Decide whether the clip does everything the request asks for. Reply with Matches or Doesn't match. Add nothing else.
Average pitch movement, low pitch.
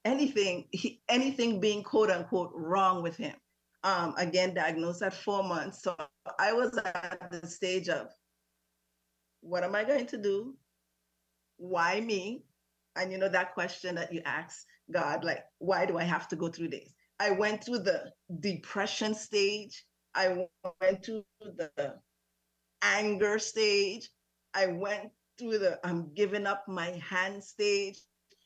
Doesn't match